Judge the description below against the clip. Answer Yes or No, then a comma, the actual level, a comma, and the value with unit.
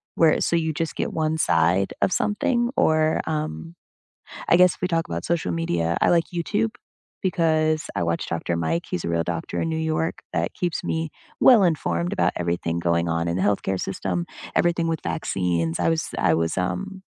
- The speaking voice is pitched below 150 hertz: Yes, medium, 140 Hz